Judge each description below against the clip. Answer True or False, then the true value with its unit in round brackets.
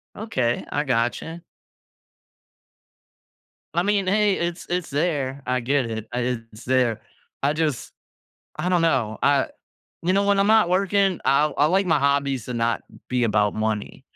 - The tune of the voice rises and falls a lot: True (6.7 semitones)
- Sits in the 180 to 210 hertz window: False (140 Hz)